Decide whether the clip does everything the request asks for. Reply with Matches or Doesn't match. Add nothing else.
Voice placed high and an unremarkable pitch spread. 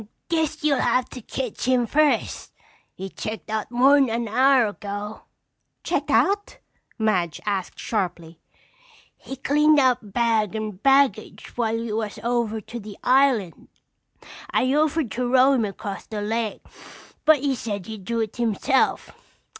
Matches